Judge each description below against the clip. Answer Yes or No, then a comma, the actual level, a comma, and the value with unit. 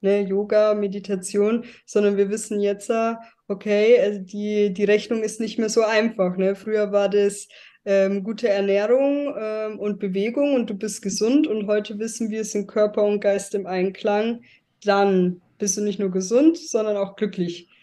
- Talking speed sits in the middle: Yes, average, 170 wpm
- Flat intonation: Yes, narrow, 1.7 semitones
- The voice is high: Yes, high, 210 Hz